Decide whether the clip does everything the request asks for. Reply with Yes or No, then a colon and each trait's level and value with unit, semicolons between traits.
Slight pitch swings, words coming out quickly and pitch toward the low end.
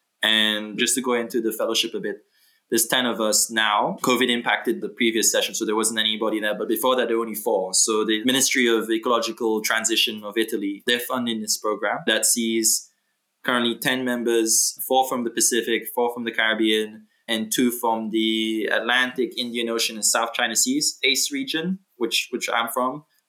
No: narrow, 2.1 semitones; average, 190 wpm; low, 115 Hz